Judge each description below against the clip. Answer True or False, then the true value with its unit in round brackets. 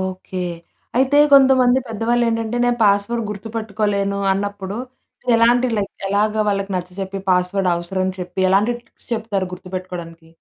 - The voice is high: True (200 Hz)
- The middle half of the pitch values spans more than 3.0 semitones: True (3.4 semitones)